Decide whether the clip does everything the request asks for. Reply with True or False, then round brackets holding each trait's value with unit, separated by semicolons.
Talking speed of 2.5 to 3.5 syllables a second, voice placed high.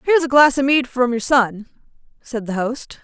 False (5.4 syllables/s; 255 Hz)